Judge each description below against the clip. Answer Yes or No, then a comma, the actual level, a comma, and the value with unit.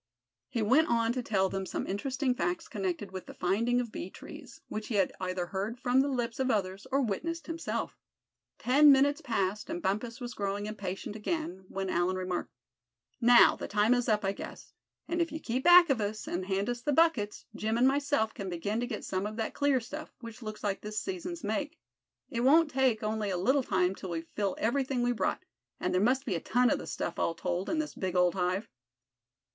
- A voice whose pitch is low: No, high, 220 Hz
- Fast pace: Yes, fast, 215 wpm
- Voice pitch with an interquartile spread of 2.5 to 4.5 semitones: No, average, 5.3 semitones